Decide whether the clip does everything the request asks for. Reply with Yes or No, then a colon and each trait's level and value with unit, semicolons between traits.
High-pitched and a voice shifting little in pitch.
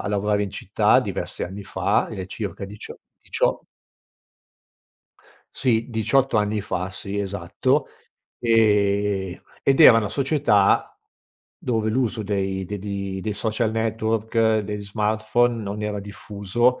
No: low, 105 Hz; narrow, 2.0 semitones